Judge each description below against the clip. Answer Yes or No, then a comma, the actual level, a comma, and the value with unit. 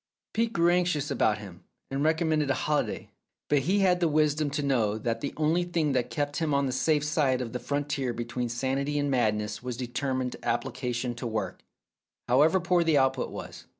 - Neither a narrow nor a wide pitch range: Yes, average, 3.9 semitones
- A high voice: No, medium, 140 Hz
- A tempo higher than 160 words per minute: Yes, average, 200 wpm